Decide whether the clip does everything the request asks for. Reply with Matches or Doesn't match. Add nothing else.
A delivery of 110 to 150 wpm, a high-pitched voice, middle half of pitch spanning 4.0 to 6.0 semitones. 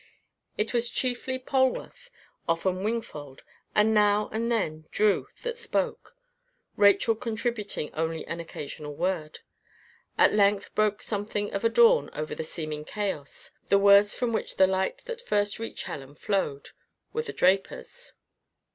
Matches